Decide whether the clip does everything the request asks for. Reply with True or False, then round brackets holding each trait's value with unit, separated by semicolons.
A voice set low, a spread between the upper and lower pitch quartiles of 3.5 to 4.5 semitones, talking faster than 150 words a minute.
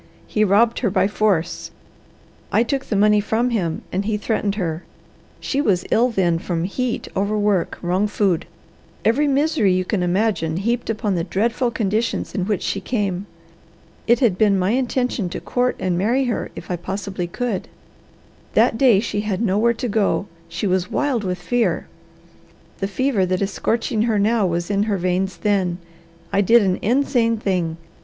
False (205 Hz; 3.9 semitones; 175 wpm)